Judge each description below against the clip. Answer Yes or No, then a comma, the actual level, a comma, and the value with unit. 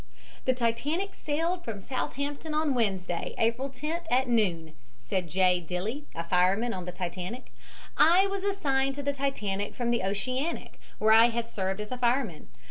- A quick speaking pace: No, average, 160 wpm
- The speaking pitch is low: No, high, 235 Hz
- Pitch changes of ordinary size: No, wide, 6.6 semitones